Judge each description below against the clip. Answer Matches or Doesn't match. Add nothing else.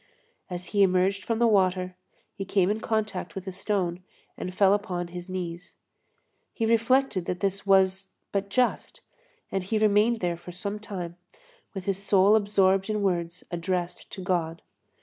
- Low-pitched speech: Doesn't match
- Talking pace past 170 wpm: Doesn't match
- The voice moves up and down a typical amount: Doesn't match